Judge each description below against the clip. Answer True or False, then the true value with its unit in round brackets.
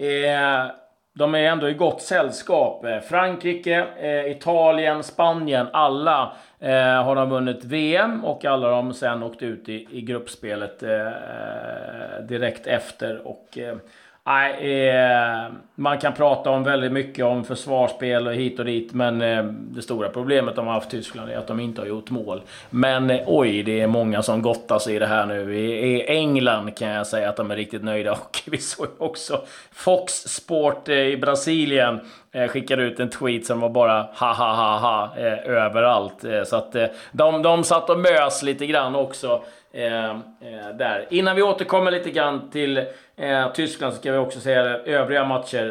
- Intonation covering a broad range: False (3.9 semitones)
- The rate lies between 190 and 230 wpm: False (165 wpm)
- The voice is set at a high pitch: False (130 Hz)